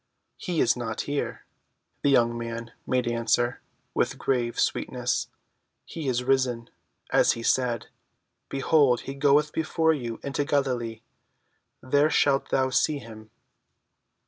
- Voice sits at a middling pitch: No, low, 130 Hz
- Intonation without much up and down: No, average, 3.2 semitones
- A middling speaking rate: No, slow, 125 wpm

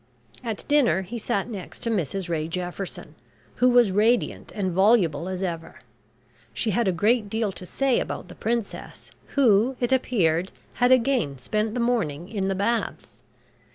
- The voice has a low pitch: No, high, 205 Hz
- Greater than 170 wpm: No, average, 160 wpm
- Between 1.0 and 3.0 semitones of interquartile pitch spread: No, average, 4.6 semitones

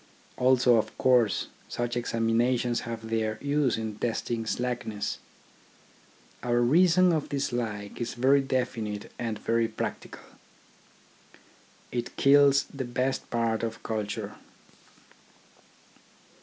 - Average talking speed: No, slow, 100 wpm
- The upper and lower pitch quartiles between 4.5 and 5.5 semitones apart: No, narrow, 2.5 semitones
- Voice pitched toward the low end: Yes, low, 120 Hz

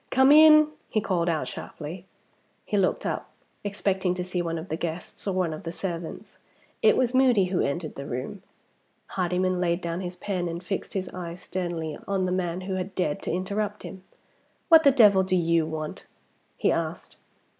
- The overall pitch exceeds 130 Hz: Yes, medium, 185 Hz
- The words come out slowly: No, average, 190 wpm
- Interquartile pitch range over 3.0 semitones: No, average, 2.7 semitones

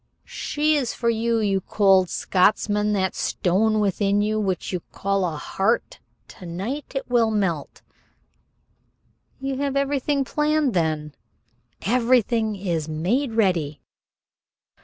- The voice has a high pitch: Yes, high, 210 Hz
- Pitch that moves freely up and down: No, average, 4.9 semitones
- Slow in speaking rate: Yes, slow, 115 wpm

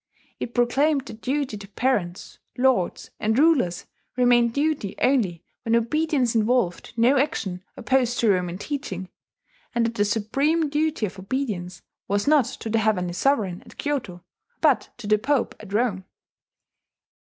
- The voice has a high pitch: Yes, high, 230 Hz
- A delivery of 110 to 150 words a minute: Yes, average, 145 wpm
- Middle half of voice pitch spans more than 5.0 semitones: Yes, wide, 5.5 semitones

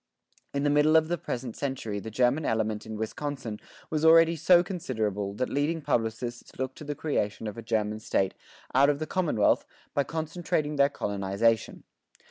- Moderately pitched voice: No, low, 130 Hz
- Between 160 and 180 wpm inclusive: Yes, average, 170 wpm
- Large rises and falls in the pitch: Yes, wide, 5.8 semitones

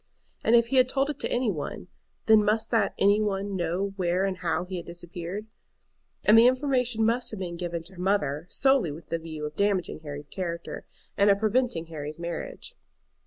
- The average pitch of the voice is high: Yes, high, 195 Hz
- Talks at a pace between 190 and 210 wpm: Yes, average, 200 wpm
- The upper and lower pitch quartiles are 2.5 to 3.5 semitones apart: No, average, 4.7 semitones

